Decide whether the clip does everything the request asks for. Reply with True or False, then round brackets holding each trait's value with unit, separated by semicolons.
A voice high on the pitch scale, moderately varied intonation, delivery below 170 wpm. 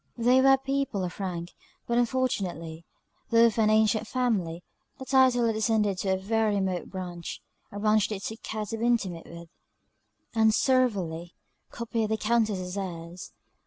True (215 Hz; 4.2 semitones; 160 wpm)